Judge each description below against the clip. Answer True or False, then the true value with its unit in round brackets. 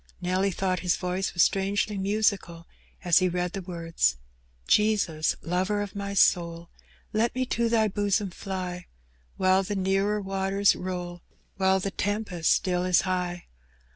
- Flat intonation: True (2.1 semitones)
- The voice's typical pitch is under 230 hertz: True (190 Hz)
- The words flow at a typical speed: True (150 wpm)